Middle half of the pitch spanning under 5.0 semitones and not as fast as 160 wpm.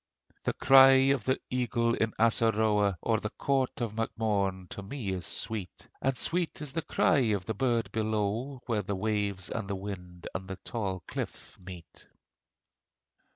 No: average, 3.9 semitones; average, 165 wpm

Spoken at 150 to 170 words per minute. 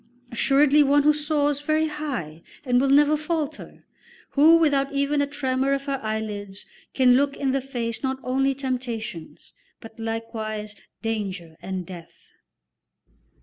No: average, 140 wpm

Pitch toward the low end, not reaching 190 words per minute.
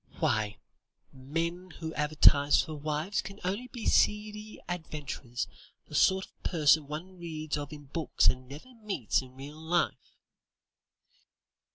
No: medium, 155 Hz; slow, 135 wpm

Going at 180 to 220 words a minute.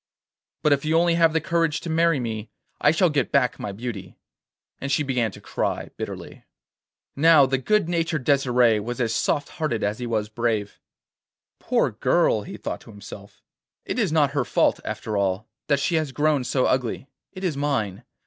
Yes: average, 185 wpm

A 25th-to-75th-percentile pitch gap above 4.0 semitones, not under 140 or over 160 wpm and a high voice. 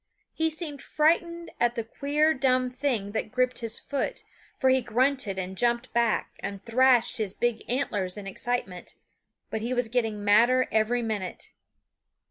No: average, 3.3 semitones; average, 155 wpm; high, 240 Hz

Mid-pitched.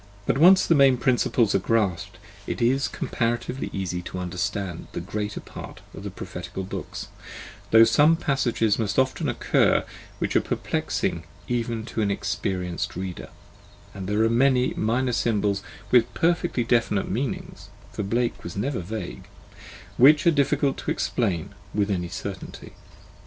No: low, 115 Hz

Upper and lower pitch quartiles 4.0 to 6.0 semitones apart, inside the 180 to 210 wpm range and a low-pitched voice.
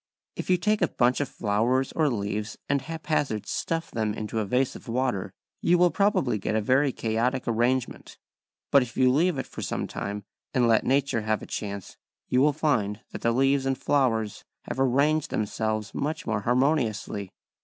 Yes: average, 4.5 semitones; average, 185 wpm; low, 125 Hz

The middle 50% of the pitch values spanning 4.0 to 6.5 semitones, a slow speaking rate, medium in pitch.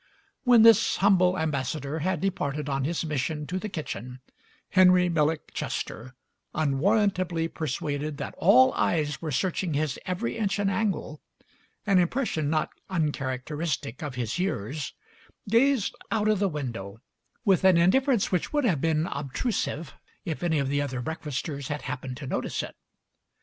No: average, 4.9 semitones; average, 155 wpm; medium, 160 Hz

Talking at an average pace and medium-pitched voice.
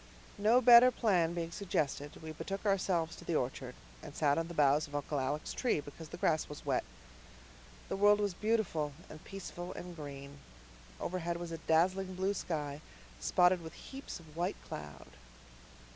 Yes: average, 170 wpm; medium, 170 Hz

